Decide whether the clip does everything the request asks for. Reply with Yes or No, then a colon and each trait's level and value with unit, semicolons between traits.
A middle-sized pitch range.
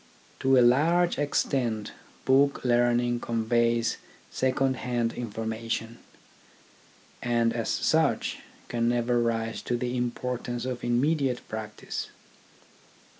No: narrow, 1.6 semitones